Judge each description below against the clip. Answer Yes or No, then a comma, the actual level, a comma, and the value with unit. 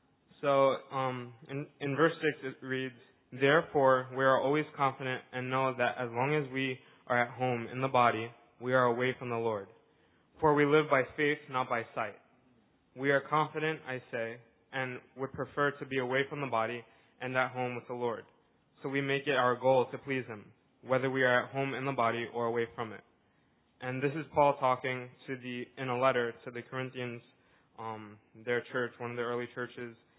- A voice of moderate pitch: No, low, 130 Hz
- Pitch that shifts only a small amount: Yes, narrow, 2.2 semitones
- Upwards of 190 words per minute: Yes, fast, 205 wpm